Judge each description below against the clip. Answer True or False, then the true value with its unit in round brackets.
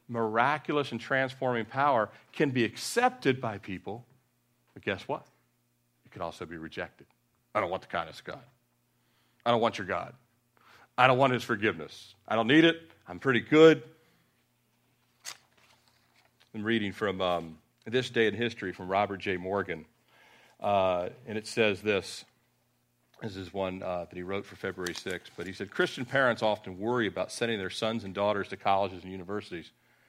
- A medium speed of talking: True (170 wpm)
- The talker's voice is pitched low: True (110 Hz)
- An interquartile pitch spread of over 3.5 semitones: True (4.3 semitones)